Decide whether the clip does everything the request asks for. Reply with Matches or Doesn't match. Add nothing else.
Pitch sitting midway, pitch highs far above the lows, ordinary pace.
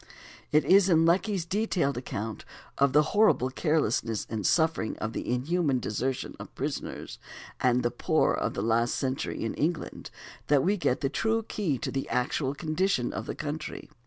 Matches